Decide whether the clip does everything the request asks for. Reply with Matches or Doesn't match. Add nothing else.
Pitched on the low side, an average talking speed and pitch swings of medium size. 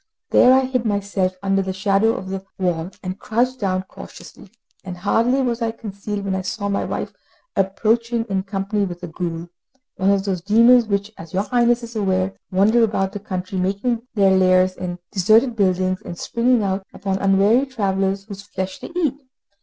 Doesn't match